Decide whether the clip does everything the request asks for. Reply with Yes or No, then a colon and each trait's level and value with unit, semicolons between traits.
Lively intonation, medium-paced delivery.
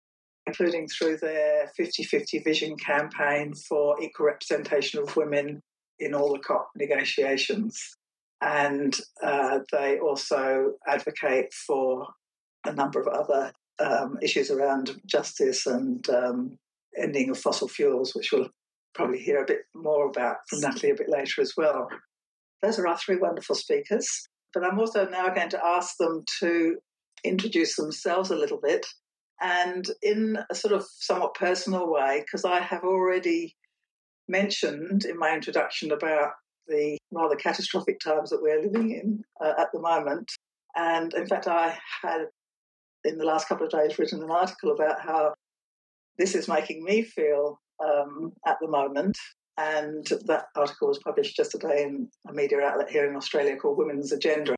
Yes: wide, 7.2 semitones; average, 155 wpm